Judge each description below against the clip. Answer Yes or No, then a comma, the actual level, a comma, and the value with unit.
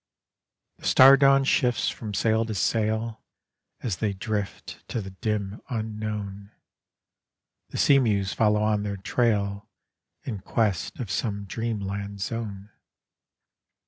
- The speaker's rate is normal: No, slow, 120 wpm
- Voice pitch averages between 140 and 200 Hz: No, low, 105 Hz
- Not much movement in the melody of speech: Yes, narrow, 2.2 semitones